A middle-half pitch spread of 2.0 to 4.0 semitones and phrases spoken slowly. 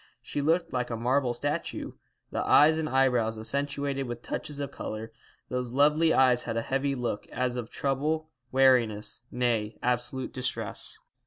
No: average, 2.9 semitones; average, 155 wpm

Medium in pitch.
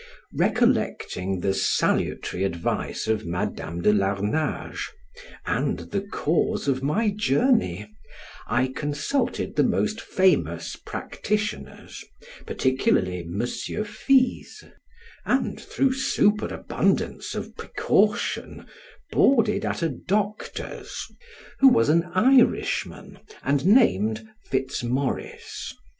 Yes: medium, 145 Hz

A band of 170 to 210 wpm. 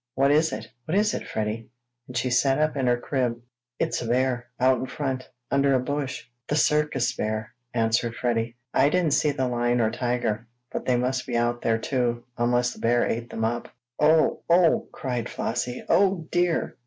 Yes: average, 190 wpm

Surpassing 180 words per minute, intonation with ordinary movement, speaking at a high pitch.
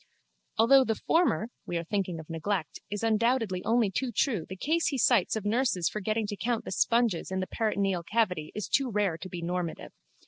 Yes: average, 200 wpm; average, 4.2 semitones; high, 210 Hz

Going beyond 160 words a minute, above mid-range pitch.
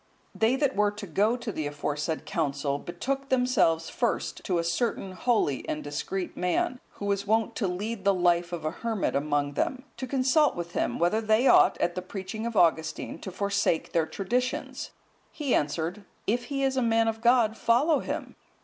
Yes: average, 185 wpm; high, 200 Hz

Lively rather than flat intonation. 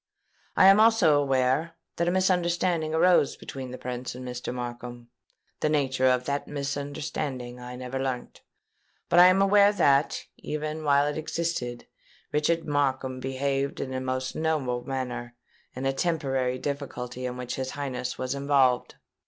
No: average, 3.5 semitones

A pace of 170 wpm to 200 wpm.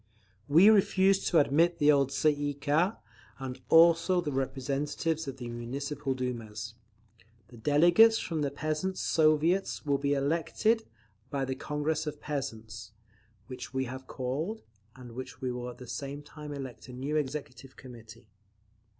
No: average, 150 wpm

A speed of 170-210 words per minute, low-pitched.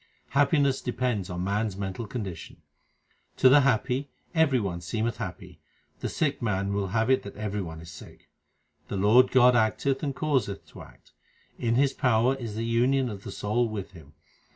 Yes: average, 180 wpm; low, 115 Hz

